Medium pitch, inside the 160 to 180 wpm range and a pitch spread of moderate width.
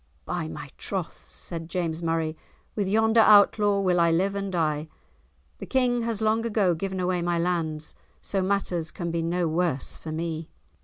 Yes: medium, 175 Hz; average, 170 wpm; average, 3.5 semitones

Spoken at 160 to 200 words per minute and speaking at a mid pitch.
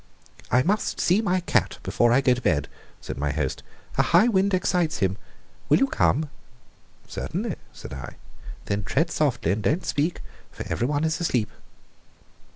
Yes: average, 165 wpm; medium, 145 Hz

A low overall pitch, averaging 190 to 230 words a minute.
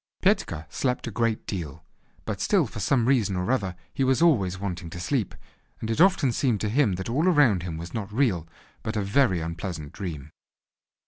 Yes: low, 105 Hz; average, 195 wpm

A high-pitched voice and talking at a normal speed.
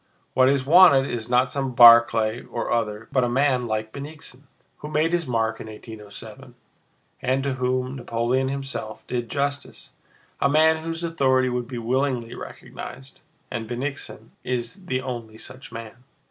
No: low, 130 Hz; average, 150 wpm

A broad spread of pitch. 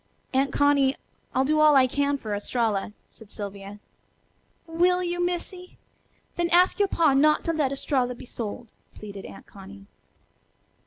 Yes: wide, 7.1 semitones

